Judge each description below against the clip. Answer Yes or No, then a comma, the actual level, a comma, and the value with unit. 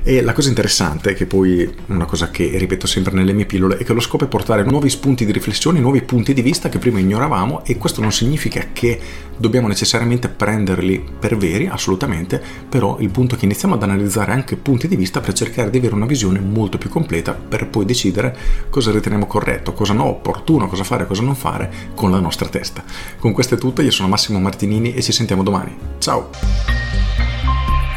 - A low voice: Yes, low, 105 Hz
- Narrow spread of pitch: No, average, 4.7 semitones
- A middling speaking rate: No, fast, 200 wpm